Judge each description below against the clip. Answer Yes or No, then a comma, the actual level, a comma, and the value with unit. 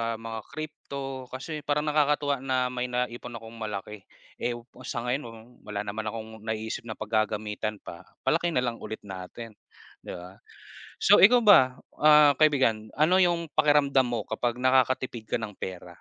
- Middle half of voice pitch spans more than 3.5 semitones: Yes, average, 4.7 semitones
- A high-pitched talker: No, low, 125 Hz